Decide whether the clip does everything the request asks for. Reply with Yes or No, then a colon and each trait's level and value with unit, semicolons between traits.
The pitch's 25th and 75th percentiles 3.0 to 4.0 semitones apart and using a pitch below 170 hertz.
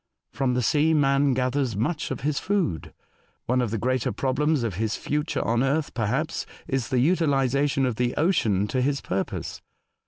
Yes: average, 3.3 semitones; low, 135 Hz